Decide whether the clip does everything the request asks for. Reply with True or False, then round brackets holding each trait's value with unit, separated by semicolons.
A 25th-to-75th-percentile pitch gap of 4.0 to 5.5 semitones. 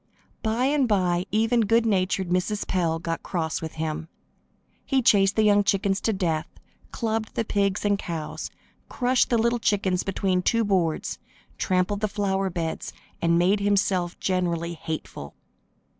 False (3.6 semitones)